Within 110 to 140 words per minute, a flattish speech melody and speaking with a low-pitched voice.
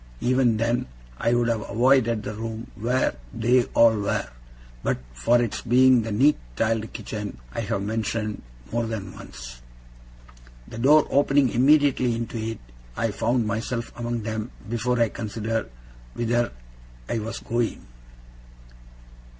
Yes: slow, 135 wpm; narrow, 1.8 semitones; low, 115 Hz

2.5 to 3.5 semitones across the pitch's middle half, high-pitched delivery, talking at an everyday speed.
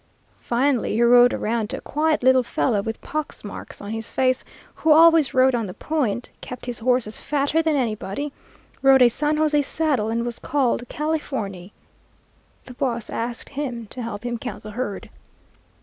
No: average, 4.2 semitones; very high, 250 Hz; average, 175 wpm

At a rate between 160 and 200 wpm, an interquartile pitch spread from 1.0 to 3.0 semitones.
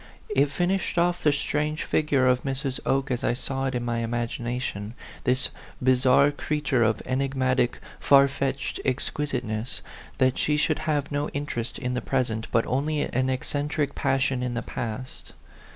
Yes: average, 170 wpm; narrow, 2.5 semitones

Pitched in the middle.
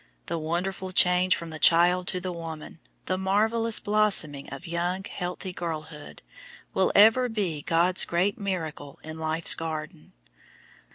Yes: medium, 175 Hz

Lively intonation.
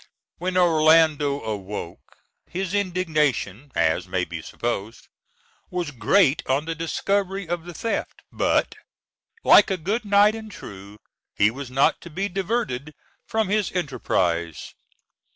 Yes: wide, 7.5 semitones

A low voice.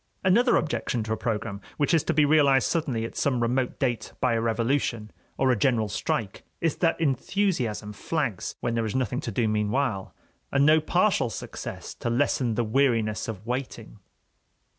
Yes: low, 125 Hz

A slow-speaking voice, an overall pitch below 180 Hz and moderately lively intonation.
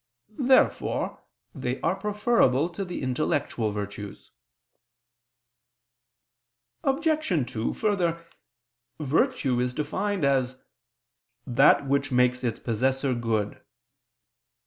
No: slow, 85 wpm; medium, 140 Hz; wide, 6.9 semitones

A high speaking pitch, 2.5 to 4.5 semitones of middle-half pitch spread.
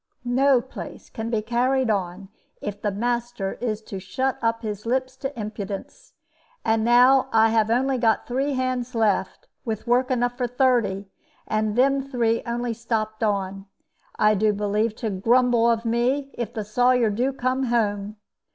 Yes: high, 235 Hz; average, 2.9 semitones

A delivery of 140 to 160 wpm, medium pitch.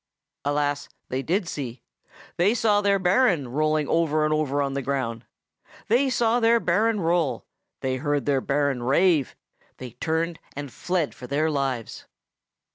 Yes: average, 150 wpm; medium, 155 Hz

